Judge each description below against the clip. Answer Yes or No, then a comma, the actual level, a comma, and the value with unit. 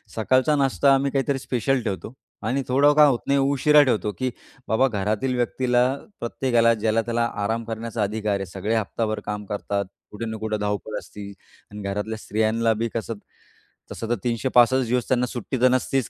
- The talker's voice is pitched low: Yes, low, 115 Hz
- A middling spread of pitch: Yes, average, 3.2 semitones